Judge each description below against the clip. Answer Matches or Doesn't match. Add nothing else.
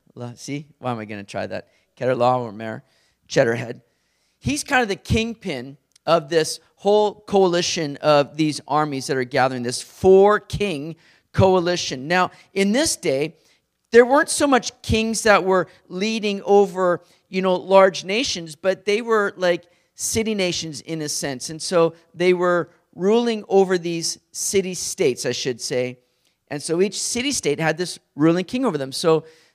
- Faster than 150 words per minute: Matches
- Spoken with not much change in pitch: Doesn't match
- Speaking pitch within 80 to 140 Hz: Doesn't match